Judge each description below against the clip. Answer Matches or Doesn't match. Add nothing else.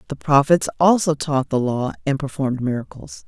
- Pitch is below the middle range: Doesn't match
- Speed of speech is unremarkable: Matches